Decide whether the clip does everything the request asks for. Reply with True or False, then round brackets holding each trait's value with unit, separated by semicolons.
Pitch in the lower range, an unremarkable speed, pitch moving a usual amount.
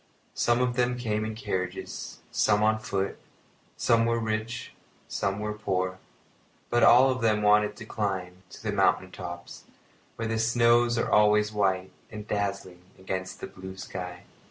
True (105 Hz; 155 wpm; 3.2 semitones)